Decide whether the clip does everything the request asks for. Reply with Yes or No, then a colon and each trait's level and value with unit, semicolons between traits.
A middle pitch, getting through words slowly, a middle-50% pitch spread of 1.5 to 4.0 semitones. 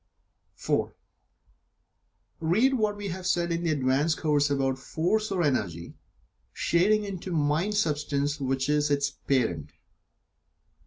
No: medium, 150 Hz; slow, 120 wpm; average, 4.8 semitones